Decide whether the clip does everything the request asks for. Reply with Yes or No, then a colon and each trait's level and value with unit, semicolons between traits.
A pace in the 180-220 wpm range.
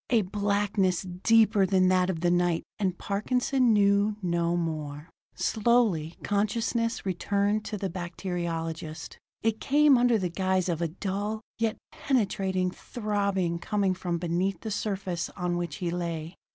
No: average, 140 wpm